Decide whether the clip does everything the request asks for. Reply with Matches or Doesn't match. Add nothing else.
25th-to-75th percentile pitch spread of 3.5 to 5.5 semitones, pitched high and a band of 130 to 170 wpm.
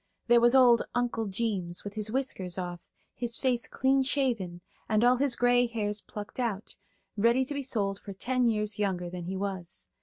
Doesn't match